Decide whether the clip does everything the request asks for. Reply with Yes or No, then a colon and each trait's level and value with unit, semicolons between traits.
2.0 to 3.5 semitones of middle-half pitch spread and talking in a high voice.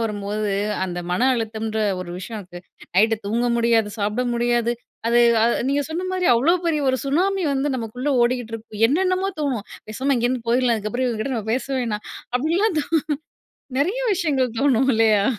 No: average, 4.3 semitones; high, 240 Hz